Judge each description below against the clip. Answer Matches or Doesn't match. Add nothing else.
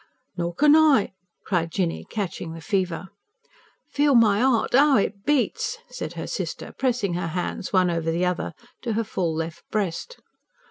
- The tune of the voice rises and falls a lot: Matches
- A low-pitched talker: Doesn't match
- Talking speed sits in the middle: Matches